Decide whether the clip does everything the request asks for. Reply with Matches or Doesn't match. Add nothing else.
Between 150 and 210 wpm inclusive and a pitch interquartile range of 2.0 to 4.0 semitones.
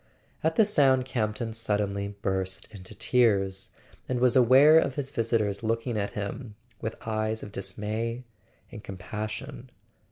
Doesn't match